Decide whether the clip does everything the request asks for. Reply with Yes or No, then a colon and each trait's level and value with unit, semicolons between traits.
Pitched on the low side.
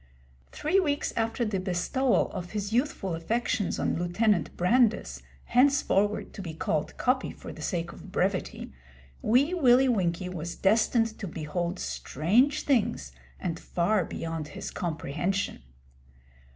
No: high, 195 Hz